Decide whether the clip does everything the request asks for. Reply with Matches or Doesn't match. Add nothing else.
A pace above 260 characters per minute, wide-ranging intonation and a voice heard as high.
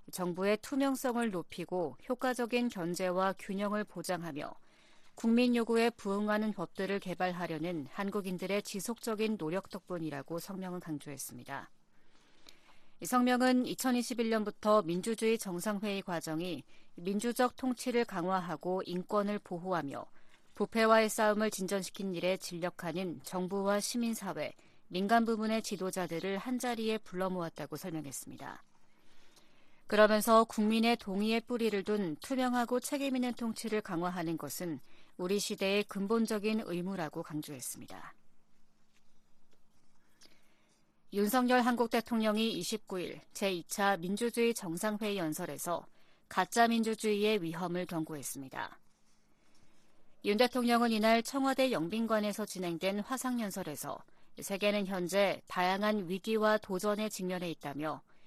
Doesn't match